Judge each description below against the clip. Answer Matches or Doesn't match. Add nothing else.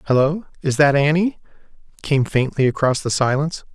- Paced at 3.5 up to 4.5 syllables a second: Doesn't match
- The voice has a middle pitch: Matches